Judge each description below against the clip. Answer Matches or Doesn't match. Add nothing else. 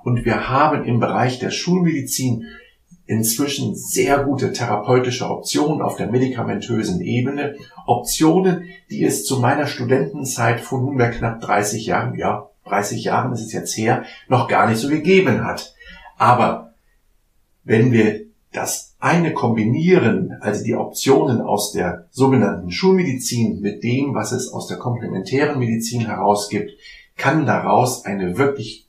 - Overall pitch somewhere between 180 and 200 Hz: Doesn't match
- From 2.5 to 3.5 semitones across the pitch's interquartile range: Doesn't match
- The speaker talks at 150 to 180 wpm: Doesn't match